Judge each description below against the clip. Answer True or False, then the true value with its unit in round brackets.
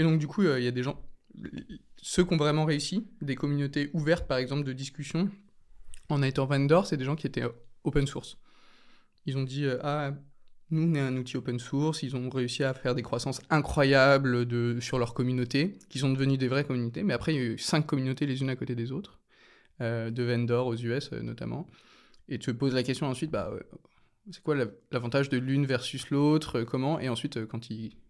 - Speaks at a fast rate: True (225 wpm)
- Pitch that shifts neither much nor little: True (3.0 semitones)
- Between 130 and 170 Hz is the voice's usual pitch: True (135 Hz)